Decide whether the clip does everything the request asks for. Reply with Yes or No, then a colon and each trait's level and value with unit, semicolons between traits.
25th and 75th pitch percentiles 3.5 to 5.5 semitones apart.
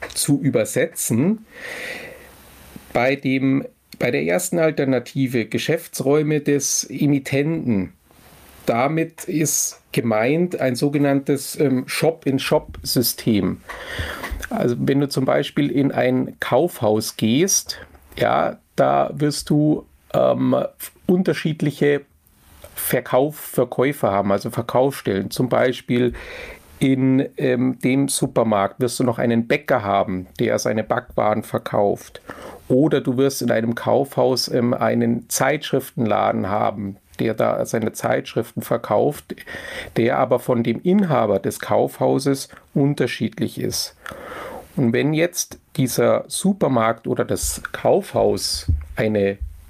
Yes: average, 4.5 semitones